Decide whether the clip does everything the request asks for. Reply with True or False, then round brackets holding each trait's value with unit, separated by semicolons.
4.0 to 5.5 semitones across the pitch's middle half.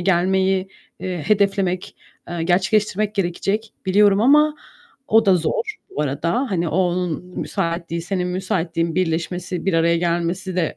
False (2.6 semitones)